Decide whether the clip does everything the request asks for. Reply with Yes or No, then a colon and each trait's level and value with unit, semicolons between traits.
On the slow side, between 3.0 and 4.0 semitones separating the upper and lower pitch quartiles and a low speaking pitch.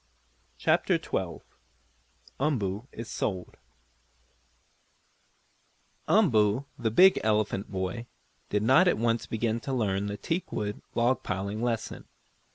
Yes: slow, 105 wpm; average, 3.5 semitones; low, 110 Hz